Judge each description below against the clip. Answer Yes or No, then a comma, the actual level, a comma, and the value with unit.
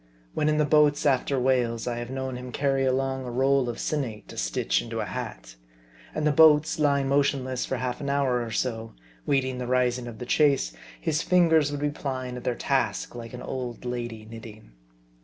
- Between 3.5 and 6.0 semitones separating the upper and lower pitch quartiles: No, average, 2.8 semitones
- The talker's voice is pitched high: No, low, 130 Hz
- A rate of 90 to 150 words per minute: No, average, 200 wpm